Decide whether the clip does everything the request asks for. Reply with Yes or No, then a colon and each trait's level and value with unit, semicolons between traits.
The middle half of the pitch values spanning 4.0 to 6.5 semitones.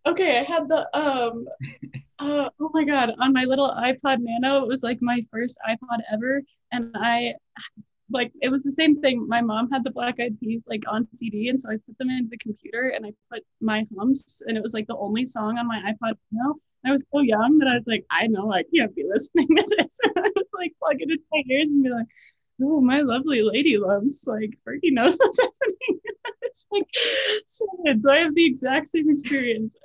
Yes: average, 4.8 semitones